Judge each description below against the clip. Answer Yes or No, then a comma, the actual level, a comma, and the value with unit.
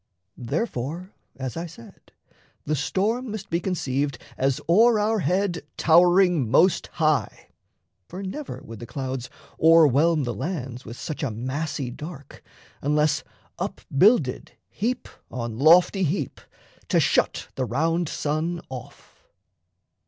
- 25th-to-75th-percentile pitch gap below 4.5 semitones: No, average, 5.3 semitones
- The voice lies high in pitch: No, medium, 160 Hz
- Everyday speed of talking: No, slow, 125 wpm